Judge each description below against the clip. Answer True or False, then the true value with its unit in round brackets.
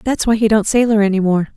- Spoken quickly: True (270 wpm)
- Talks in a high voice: True (210 Hz)